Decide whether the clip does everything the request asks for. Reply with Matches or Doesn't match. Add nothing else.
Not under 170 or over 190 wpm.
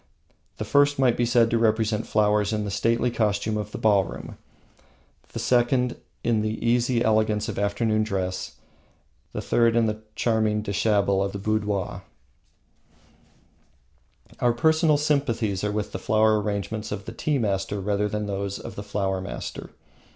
Doesn't match